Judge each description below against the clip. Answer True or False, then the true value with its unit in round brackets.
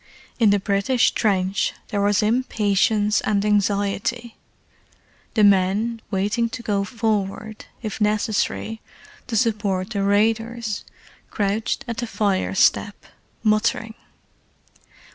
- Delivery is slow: True (105 wpm)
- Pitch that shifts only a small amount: True (2.0 semitones)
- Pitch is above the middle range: True (210 Hz)